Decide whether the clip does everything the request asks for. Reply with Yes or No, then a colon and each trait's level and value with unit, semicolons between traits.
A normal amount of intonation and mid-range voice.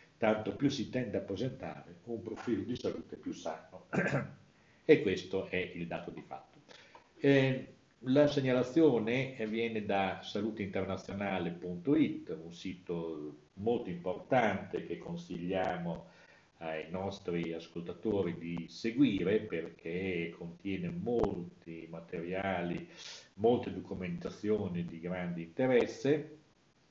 No: average, 4.8 semitones; very low, 95 Hz